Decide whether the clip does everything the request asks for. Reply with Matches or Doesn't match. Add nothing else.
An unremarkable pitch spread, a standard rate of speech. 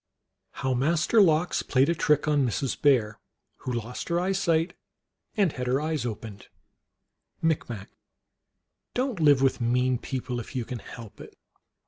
Matches